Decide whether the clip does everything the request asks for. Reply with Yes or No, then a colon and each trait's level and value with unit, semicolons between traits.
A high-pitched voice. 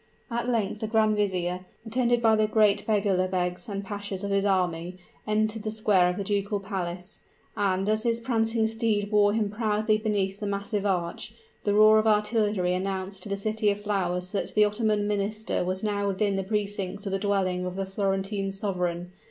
Yes: high, 205 Hz